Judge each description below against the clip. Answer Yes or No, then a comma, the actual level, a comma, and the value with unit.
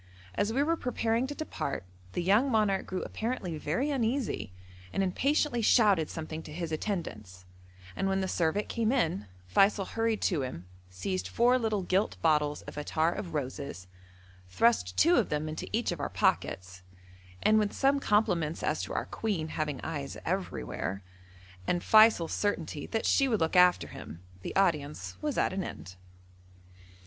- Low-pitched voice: No, medium, 180 Hz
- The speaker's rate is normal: Yes, average, 165 wpm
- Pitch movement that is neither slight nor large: No, wide, 6.7 semitones